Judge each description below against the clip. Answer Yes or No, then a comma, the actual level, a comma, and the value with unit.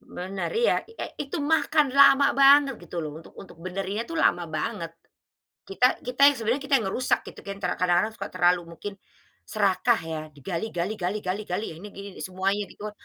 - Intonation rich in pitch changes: Yes, wide, 6.0 semitones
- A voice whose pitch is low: No, high, 205 Hz